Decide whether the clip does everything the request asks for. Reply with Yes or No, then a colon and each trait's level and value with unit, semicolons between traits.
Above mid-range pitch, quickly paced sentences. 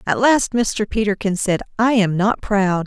No: high, 205 Hz; average, 190 wpm